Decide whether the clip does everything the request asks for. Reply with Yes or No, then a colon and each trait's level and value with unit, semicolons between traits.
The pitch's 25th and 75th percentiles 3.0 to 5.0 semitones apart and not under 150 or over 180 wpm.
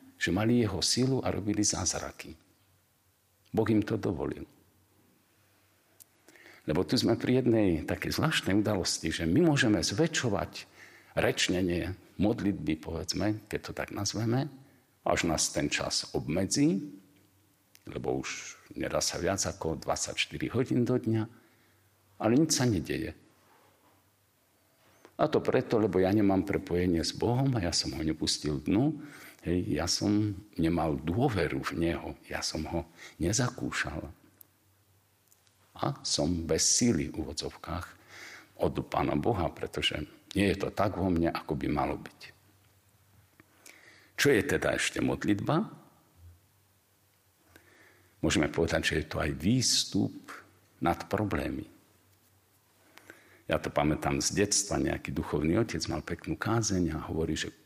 No: average, 3.5 semitones; average, 130 wpm